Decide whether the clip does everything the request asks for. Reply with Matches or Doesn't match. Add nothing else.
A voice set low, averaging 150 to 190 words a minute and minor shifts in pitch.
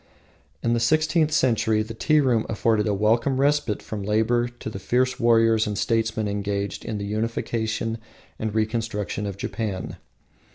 Matches